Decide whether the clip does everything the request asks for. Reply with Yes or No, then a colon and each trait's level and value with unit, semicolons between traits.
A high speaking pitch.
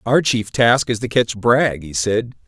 No: low, 115 Hz